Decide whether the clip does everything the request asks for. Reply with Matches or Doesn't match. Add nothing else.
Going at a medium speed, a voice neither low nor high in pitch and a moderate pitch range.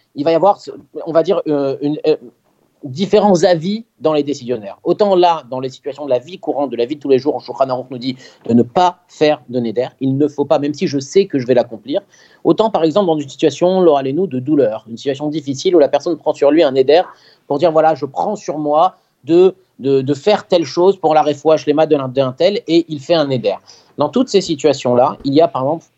Doesn't match